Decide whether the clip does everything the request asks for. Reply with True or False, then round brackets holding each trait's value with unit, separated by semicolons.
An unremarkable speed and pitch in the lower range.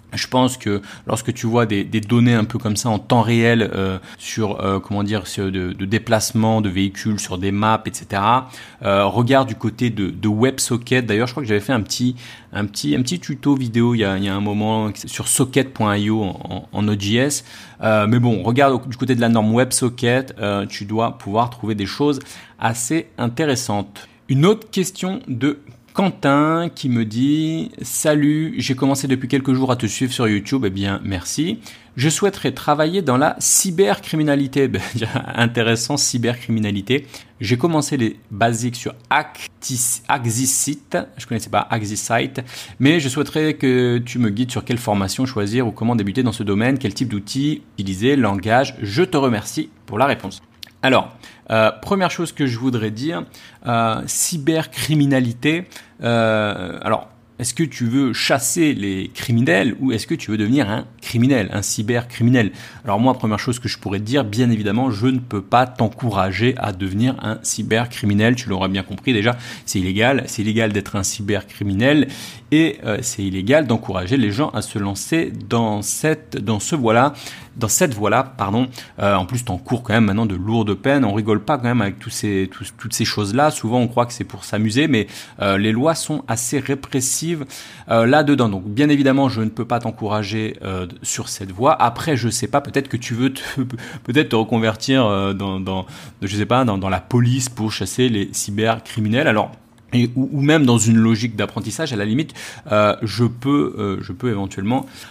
True (190 wpm; 115 Hz)